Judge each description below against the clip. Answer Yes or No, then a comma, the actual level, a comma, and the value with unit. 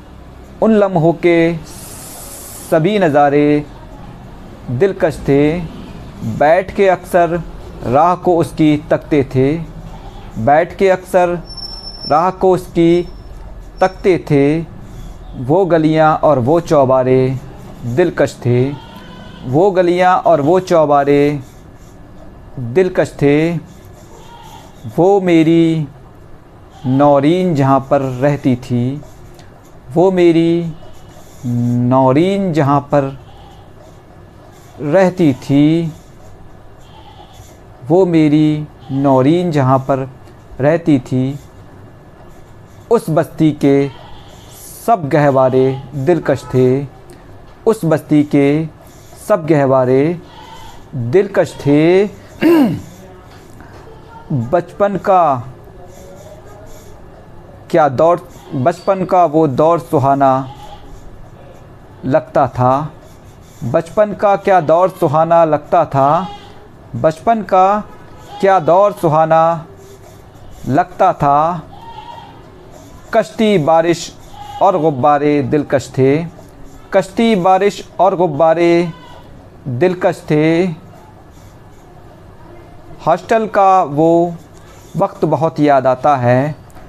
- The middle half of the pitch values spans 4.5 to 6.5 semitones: Yes, average, 5.2 semitones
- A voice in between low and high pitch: Yes, medium, 150 Hz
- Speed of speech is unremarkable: No, slow, 80 wpm